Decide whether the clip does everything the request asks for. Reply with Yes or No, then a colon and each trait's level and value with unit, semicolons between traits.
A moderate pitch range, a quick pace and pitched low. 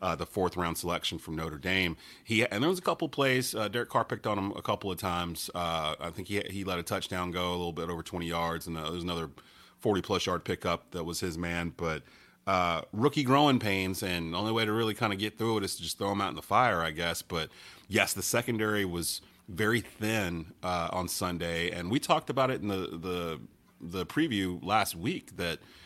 Yes: average, 3.8 semitones; fast, 240 wpm; very low, 90 Hz